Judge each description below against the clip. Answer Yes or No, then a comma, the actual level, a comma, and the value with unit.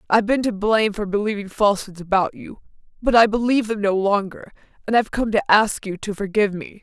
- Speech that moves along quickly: Yes, fast, 210 wpm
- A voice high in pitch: Yes, high, 205 Hz